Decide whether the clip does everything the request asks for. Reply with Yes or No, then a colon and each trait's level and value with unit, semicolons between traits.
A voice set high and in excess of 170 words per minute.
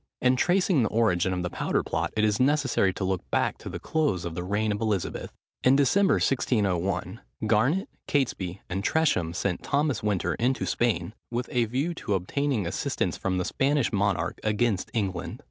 No: low, 110 Hz; average, 180 wpm